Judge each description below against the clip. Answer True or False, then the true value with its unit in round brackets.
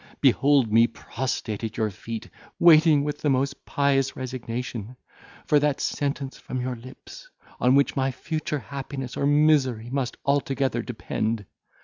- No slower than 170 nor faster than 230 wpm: False (140 wpm)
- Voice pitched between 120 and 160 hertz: True (135 Hz)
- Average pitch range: True (3.0 semitones)